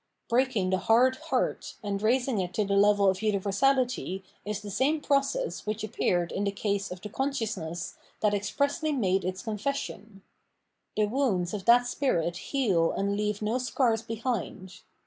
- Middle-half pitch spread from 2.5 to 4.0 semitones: No, average, 4.5 semitones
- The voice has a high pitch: Yes, high, 210 Hz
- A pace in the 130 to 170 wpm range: Yes, average, 165 wpm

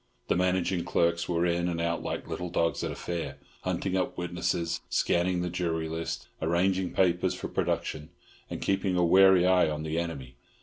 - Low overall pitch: Yes, very low, 85 Hz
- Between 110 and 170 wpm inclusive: No, average, 180 wpm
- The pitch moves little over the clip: Yes, narrow, 1.5 semitones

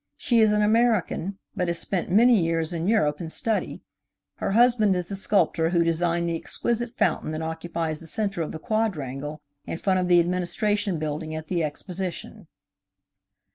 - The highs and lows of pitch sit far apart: No, average, 4.3 semitones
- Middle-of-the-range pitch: Yes, medium, 175 Hz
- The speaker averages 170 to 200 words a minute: Yes, average, 175 wpm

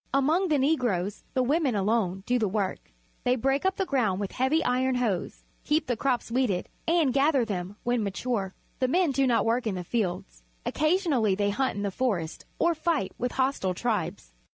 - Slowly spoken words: No, average, 195 wpm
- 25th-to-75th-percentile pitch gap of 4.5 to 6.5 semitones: Yes, wide, 5.4 semitones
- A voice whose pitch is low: No, high, 245 Hz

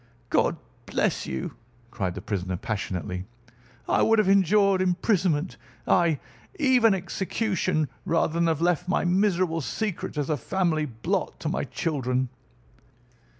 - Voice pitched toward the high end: No, medium, 170 Hz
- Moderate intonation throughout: No, wide, 5.9 semitones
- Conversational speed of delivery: No, slow, 130 wpm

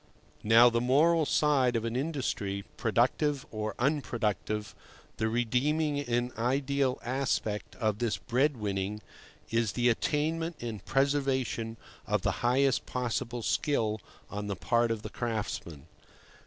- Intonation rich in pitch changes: No, average, 4.1 semitones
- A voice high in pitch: No, low, 120 Hz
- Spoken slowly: Yes, slow, 130 wpm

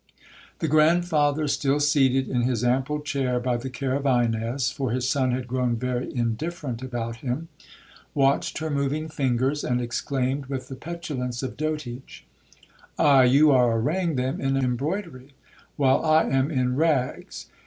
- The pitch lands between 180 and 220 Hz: No, low, 135 Hz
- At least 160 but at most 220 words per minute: No, average, 150 wpm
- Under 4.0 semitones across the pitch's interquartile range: Yes, average, 2.9 semitones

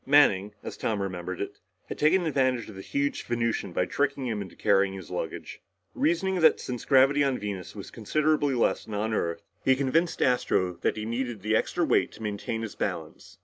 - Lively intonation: Yes, wide, 5.7 semitones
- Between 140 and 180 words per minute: No, fast, 205 wpm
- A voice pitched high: No, low, 115 Hz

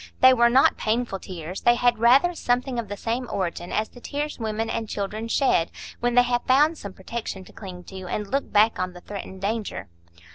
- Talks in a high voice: Yes, high, 225 Hz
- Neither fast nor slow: No, fast, 210 wpm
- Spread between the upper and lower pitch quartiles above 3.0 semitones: Yes, average, 4.1 semitones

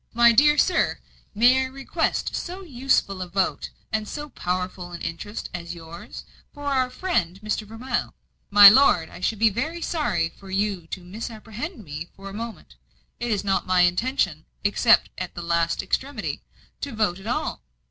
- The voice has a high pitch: Yes, high, 210 Hz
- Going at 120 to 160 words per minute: No, average, 170 wpm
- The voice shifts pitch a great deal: Yes, wide, 6.0 semitones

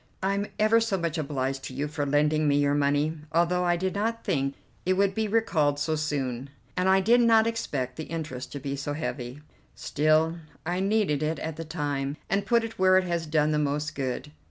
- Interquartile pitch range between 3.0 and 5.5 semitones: Yes, average, 4.6 semitones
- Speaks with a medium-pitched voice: Yes, medium, 155 Hz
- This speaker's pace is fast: Yes, fast, 210 wpm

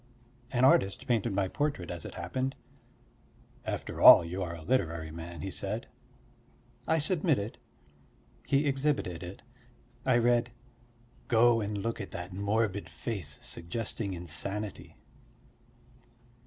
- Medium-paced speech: No, slow, 120 wpm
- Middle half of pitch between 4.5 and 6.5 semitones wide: Yes, wide, 5.4 semitones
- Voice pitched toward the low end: Yes, low, 100 Hz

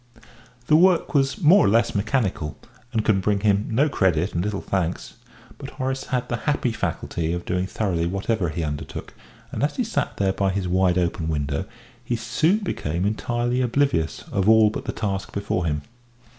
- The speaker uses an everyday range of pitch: No, wide, 5.9 semitones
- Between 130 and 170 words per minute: No, average, 185 wpm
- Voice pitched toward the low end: Yes, low, 100 Hz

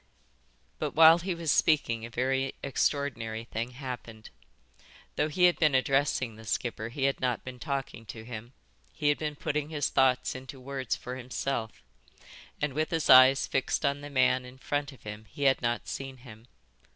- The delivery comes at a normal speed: Yes, average, 180 wpm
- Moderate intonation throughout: Yes, average, 3.2 semitones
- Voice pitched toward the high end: No, low, 130 Hz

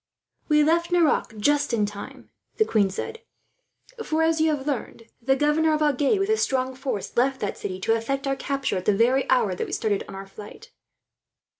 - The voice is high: Yes, very high, 270 Hz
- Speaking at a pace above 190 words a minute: Yes, average, 200 wpm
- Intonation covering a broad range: Yes, wide, 5.9 semitones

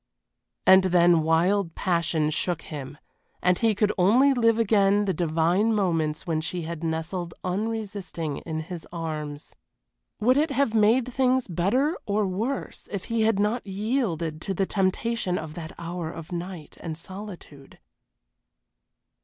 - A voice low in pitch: No, medium, 185 Hz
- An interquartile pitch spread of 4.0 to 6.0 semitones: Yes, average, 4.7 semitones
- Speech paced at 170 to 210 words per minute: No, average, 145 wpm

